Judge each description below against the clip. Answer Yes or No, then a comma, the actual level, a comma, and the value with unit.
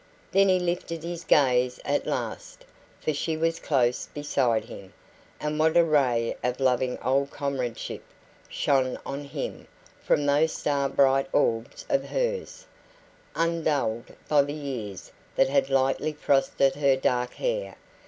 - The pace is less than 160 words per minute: Yes, average, 140 wpm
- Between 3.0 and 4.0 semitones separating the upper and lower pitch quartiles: Yes, average, 3.6 semitones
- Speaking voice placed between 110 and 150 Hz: Yes, medium, 140 Hz